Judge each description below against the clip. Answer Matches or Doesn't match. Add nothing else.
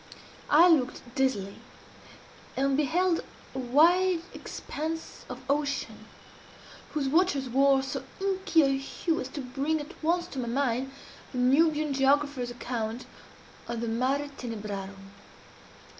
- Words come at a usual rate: Doesn't match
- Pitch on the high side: Matches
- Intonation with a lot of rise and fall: Doesn't match